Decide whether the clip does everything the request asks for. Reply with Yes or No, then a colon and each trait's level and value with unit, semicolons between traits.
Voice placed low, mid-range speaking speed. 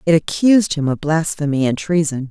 No: medium, 160 Hz; average, 180 wpm